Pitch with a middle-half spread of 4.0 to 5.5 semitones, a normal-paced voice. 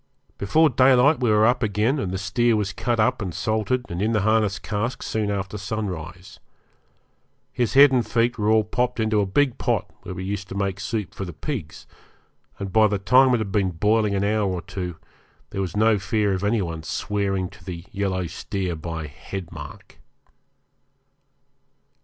No: average, 2.9 semitones; average, 190 wpm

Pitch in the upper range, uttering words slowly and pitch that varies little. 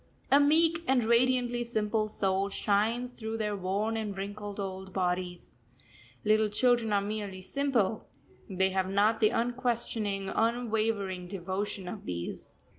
No: high, 210 Hz; slow, 130 wpm; average, 3.4 semitones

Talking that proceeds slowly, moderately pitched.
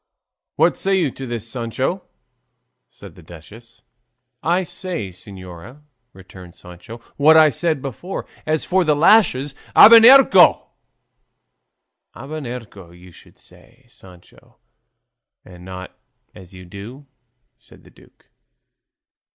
No: slow, 110 wpm; low, 120 Hz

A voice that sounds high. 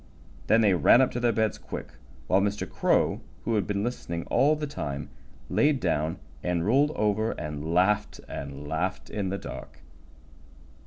No: low, 100 Hz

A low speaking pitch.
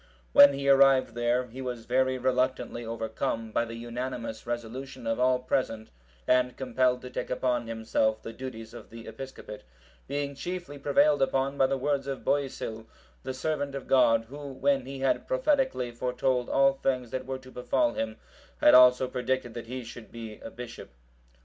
Yes: low, 130 Hz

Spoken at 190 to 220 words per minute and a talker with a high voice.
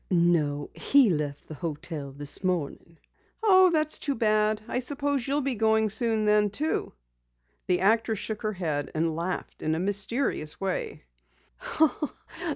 No: average, 140 wpm; high, 205 Hz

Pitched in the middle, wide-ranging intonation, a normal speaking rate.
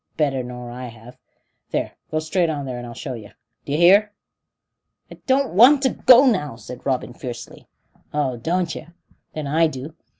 Yes: medium, 145 Hz; wide, 6.1 semitones; average, 175 wpm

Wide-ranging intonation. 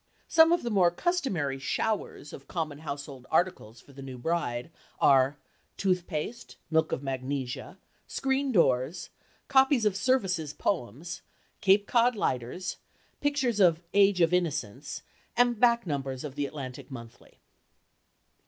Yes: wide, 7.7 semitones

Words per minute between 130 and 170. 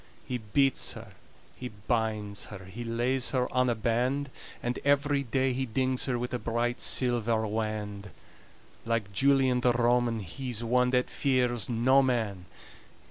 Yes: average, 150 wpm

